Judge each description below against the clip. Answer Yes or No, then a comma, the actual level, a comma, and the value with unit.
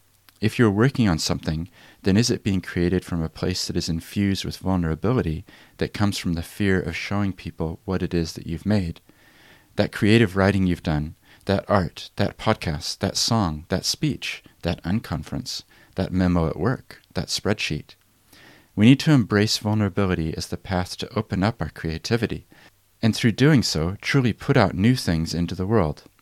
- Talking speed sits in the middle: Yes, average, 180 wpm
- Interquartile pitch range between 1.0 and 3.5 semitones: No, average, 4.0 semitones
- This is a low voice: Yes, very low, 95 Hz